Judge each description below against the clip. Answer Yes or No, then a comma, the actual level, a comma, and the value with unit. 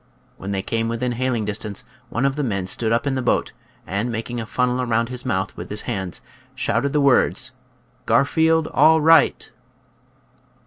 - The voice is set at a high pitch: No, low, 120 Hz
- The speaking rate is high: No, average, 180 wpm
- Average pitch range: Yes, average, 3.2 semitones